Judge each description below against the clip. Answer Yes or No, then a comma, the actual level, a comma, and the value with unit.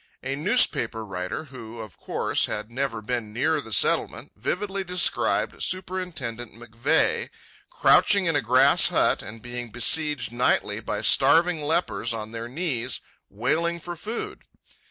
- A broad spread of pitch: Yes, wide, 6.7 semitones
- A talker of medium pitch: No, low, 130 Hz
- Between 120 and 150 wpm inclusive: Yes, slow, 135 wpm